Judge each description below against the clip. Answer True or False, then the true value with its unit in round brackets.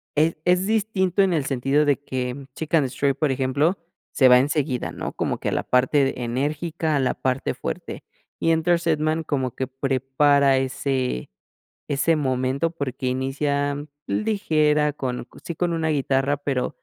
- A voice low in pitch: False (145 Hz)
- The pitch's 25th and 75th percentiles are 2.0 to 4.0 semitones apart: True (3.3 semitones)